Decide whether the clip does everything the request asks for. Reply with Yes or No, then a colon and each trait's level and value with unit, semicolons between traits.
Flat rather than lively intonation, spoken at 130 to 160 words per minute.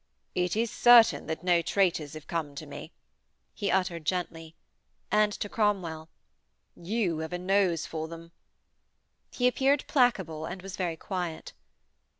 No: average, 4.0 semitones; average, 145 wpm